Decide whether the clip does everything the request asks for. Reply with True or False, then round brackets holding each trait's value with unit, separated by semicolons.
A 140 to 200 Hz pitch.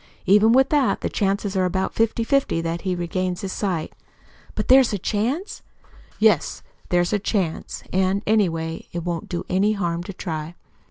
True (190 Hz)